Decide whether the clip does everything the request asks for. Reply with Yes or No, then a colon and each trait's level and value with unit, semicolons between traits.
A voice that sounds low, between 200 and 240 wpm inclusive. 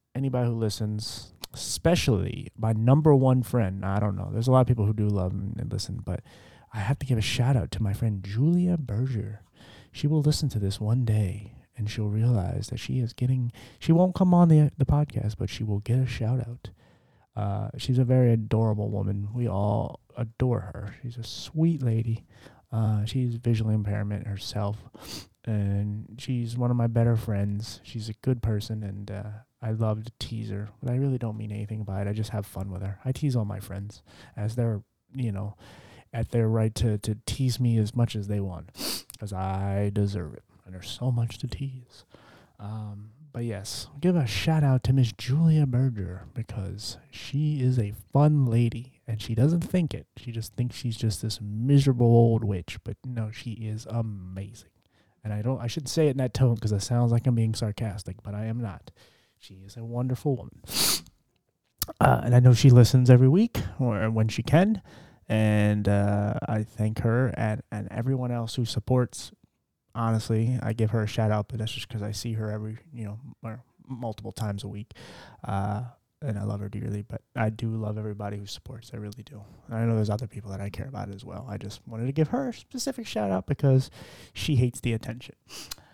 Yes: low, 115 Hz; fast, 205 wpm